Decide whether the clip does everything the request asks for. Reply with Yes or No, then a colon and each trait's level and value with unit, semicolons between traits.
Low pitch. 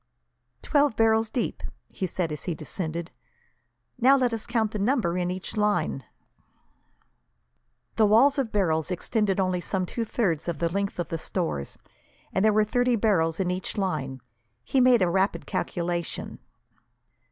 No: high, 195 Hz